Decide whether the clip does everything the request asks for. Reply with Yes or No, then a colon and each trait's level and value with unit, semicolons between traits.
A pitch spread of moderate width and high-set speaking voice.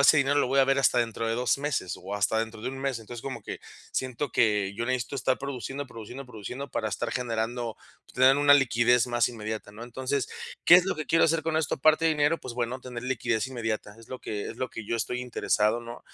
No: average, 3.3 semitones; low, 125 Hz